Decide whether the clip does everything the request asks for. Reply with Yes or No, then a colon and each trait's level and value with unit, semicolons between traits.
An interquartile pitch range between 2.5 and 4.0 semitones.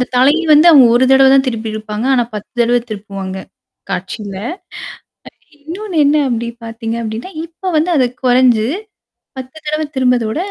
No: average, 4.4 semitones